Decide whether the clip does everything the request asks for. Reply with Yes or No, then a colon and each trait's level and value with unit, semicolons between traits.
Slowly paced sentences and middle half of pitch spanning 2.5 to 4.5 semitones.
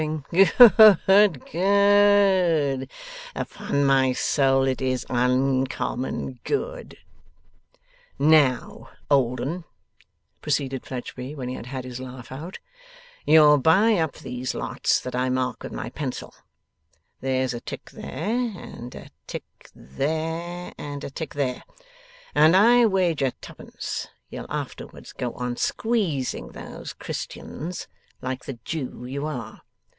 No: slow, 120 wpm; average, 5.1 semitones